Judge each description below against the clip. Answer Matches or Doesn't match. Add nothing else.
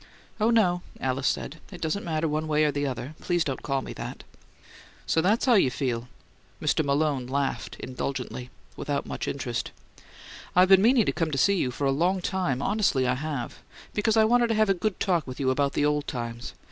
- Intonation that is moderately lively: Doesn't match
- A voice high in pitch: Doesn't match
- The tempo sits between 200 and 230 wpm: Matches